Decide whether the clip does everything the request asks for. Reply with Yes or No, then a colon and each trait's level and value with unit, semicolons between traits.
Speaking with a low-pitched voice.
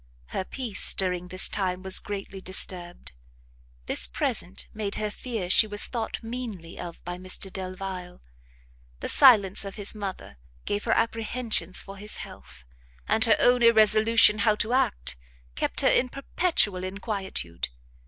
No: high, 200 Hz